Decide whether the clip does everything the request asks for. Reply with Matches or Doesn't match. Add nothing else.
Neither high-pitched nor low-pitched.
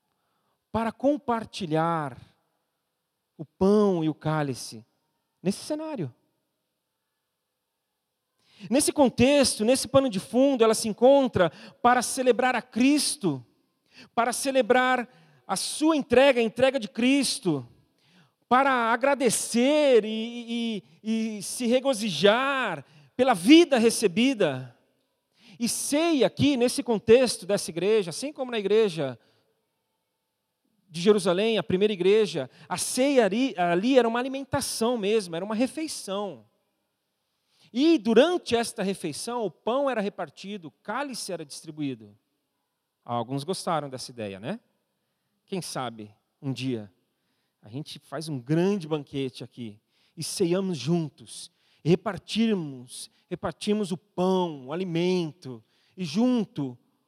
Doesn't match